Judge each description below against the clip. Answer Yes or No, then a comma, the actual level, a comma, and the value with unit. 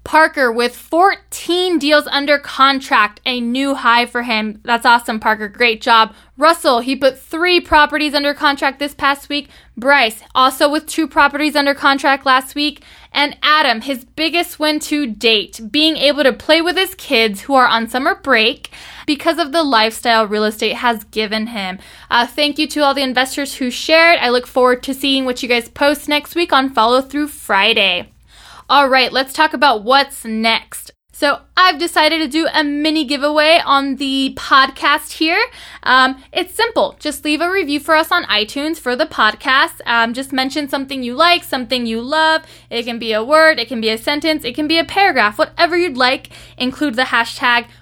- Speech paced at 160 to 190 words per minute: Yes, average, 185 wpm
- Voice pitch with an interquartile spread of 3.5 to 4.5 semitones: Yes, average, 4.2 semitones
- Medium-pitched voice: No, very high, 275 Hz